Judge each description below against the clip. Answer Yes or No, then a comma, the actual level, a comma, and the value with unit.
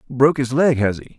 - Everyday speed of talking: No, fast, 255 wpm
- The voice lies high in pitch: No, low, 130 Hz